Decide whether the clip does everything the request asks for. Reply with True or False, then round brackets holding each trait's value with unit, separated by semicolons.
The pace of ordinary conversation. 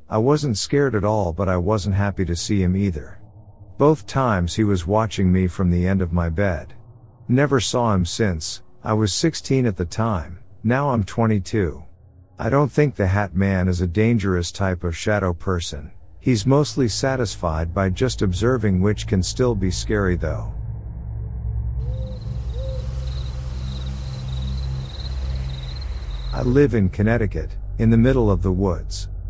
True (150 wpm)